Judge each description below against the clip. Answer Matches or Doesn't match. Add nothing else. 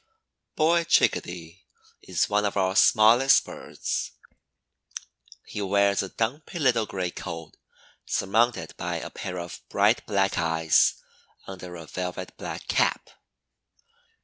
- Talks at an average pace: Doesn't match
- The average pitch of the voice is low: Matches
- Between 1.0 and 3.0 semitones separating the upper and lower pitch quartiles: Doesn't match